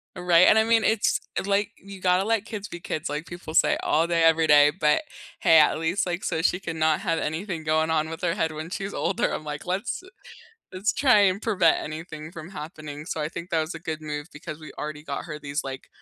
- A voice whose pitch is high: No, medium, 165 Hz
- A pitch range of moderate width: Yes, average, 3.1 semitones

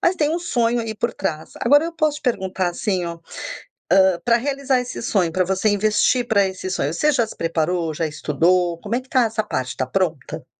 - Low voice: No, high, 200 Hz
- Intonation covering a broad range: Yes, wide, 6.1 semitones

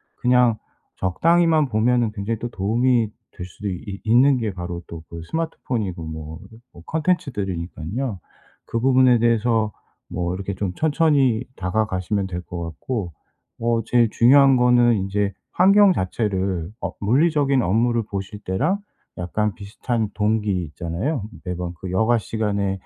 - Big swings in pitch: No, average, 4.9 semitones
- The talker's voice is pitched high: No, low, 110 Hz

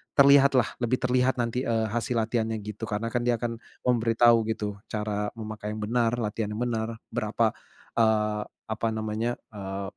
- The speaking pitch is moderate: No, low, 115 Hz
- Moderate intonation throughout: No, narrow, 2.0 semitones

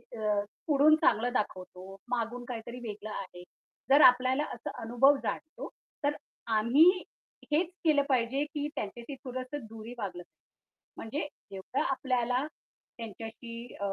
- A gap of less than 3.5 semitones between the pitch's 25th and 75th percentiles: No, average, 3.9 semitones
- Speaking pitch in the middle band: No, high, 245 Hz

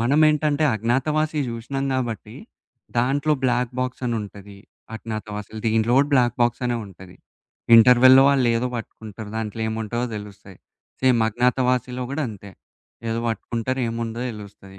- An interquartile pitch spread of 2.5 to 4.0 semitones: Yes, average, 2.8 semitones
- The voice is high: No, low, 120 Hz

